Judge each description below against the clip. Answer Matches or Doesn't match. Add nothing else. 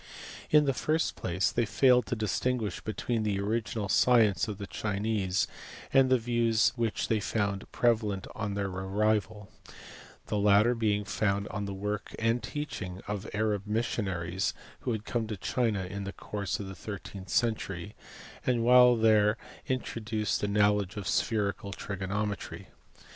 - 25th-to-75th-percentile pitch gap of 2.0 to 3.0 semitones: Matches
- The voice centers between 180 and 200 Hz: Doesn't match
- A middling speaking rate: Matches